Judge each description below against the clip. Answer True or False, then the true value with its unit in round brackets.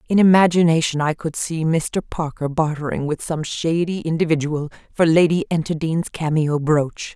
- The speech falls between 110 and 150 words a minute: True (145 wpm)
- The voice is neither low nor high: True (160 Hz)